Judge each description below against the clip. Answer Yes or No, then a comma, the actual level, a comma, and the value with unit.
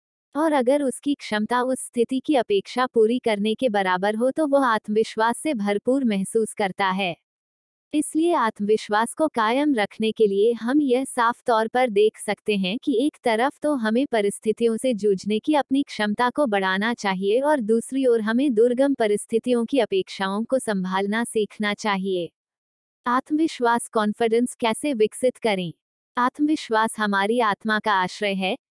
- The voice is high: Yes, high, 225 Hz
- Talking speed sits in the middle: Yes, average, 150 wpm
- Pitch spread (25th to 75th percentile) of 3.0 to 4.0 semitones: Yes, average, 3.5 semitones